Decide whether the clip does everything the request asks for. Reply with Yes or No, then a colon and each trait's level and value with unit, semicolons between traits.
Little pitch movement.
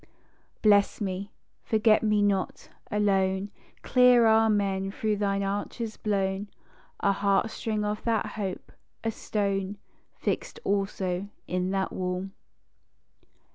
Yes: narrow, 1.7 semitones